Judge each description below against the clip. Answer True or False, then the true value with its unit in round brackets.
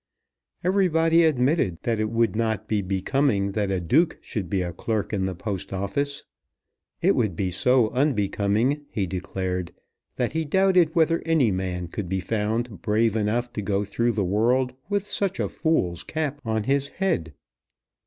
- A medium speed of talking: True (165 wpm)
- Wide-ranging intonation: True (6.6 semitones)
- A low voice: True (110 Hz)